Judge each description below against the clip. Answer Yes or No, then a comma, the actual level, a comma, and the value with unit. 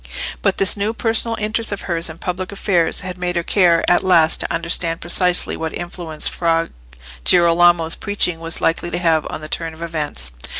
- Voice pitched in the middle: Yes, medium, 170 Hz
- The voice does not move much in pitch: Yes, narrow, 1.9 semitones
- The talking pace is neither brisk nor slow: Yes, average, 185 wpm